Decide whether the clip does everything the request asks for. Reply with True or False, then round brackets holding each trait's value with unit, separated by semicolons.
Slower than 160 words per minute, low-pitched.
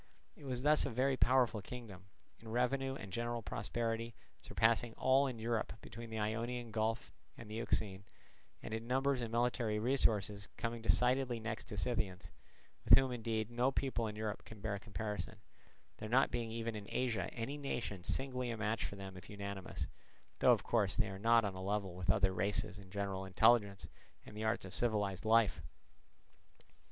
False (180 wpm; 115 Hz)